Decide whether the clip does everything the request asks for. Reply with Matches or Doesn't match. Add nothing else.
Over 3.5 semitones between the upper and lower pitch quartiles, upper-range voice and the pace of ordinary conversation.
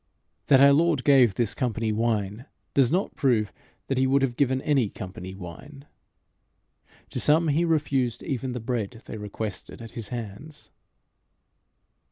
Doesn't match